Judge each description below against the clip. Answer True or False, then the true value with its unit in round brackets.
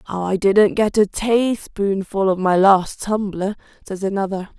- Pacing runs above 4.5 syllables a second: False (3.9 syllables/s)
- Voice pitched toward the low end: False (200 Hz)